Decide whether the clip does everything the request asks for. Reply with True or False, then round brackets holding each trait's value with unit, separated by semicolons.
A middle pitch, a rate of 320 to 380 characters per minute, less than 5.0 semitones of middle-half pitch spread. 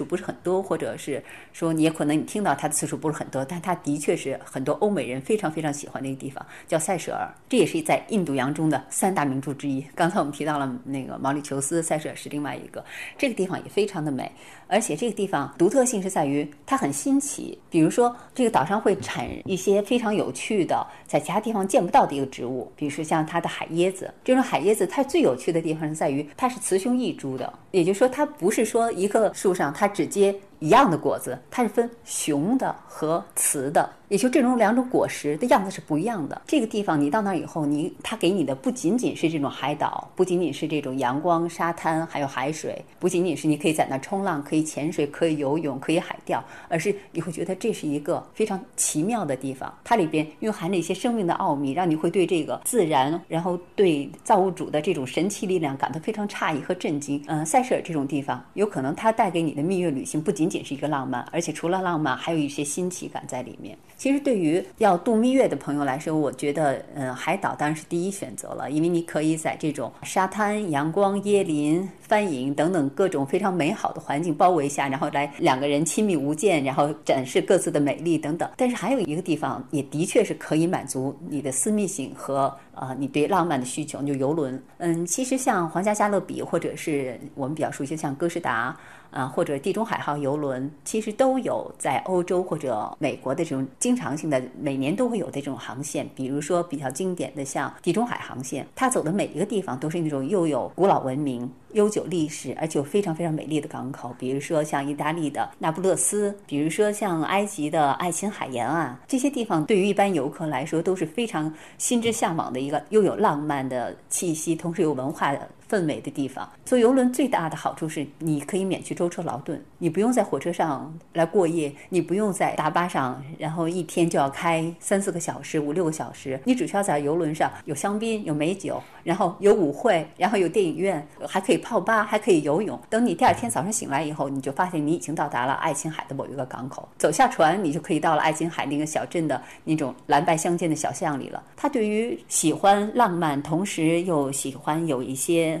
False (160 Hz; 340 characters per minute; 5.3 semitones)